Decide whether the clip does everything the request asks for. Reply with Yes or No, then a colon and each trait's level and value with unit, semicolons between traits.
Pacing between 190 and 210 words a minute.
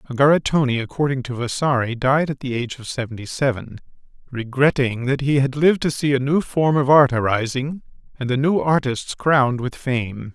No: average, 180 wpm